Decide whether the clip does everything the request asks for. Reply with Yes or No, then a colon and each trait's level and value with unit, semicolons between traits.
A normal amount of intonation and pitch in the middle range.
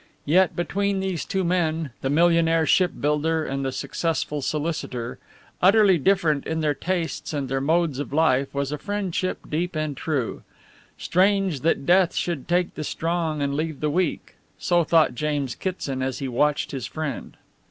Yes: average, 3.6 semitones; medium, 160 Hz